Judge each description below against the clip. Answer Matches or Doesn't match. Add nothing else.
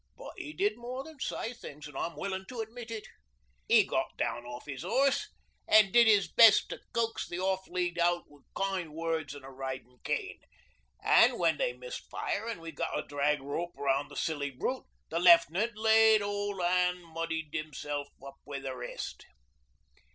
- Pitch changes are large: Matches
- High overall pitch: Doesn't match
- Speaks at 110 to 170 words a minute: Doesn't match